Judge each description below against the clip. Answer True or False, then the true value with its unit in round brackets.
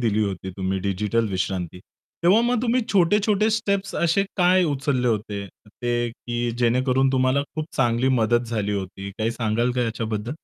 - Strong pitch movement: True (6.7 semitones)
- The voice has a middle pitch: False (120 Hz)